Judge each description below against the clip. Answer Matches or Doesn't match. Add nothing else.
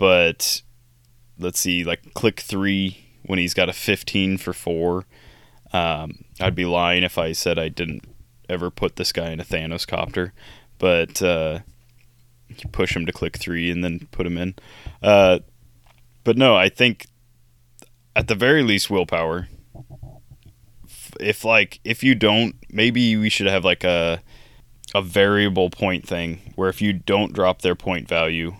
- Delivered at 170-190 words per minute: Doesn't match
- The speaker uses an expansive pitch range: Doesn't match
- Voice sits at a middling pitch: Doesn't match